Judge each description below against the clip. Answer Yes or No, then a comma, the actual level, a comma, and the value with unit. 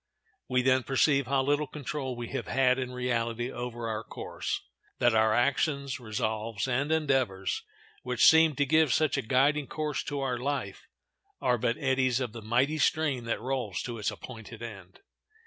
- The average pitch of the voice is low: Yes, low, 130 Hz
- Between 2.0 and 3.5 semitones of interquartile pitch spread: Yes, average, 3.1 semitones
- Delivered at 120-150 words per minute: No, average, 170 wpm